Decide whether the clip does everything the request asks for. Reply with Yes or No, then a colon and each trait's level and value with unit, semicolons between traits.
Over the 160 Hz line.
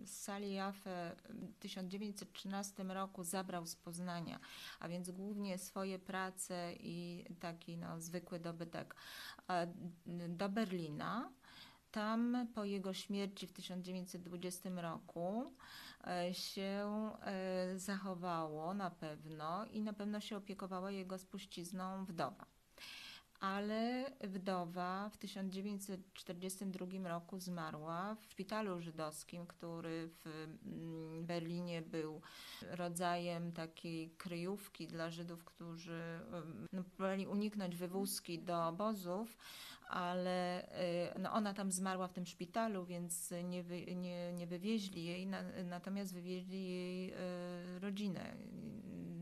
Yes: medium, 185 Hz